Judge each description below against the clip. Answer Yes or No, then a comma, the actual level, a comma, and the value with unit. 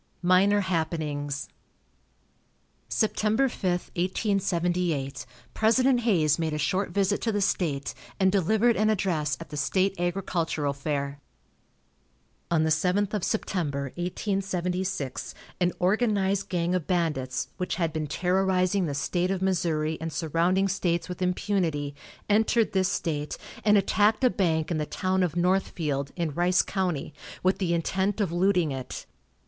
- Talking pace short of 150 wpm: Yes, average, 140 wpm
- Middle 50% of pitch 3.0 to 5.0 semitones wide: Yes, average, 3.7 semitones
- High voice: No, medium, 180 Hz